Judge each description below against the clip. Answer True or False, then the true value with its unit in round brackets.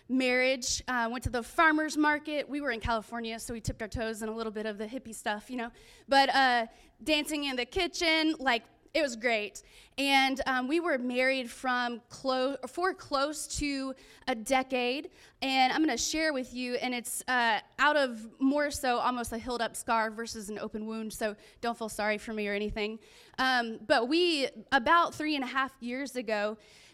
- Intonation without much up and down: False (3.4 semitones)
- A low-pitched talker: False (255 Hz)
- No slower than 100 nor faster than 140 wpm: False (200 wpm)